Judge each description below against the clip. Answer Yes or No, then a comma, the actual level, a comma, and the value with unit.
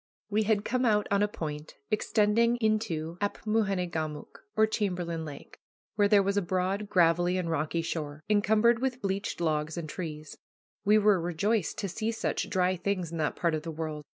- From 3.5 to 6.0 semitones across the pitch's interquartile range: Yes, average, 4.4 semitones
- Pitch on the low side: No, medium, 185 Hz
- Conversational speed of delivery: Yes, average, 180 wpm